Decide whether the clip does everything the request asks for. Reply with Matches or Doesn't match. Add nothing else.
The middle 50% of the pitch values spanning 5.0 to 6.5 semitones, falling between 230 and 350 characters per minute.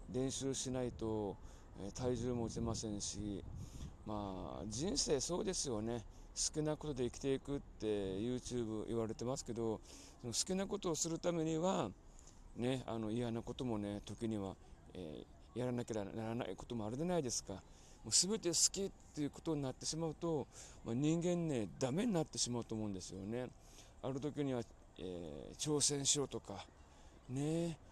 Matches